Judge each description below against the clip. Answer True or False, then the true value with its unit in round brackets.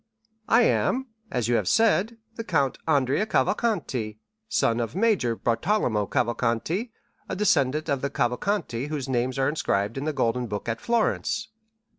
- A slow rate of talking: False (150 wpm)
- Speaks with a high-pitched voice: False (140 Hz)